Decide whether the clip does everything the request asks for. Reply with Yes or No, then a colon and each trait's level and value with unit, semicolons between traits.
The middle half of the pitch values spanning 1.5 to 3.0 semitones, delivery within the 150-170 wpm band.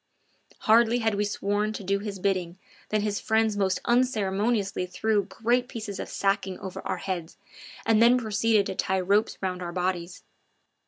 Yes: average, 2.7 semitones; average, 165 wpm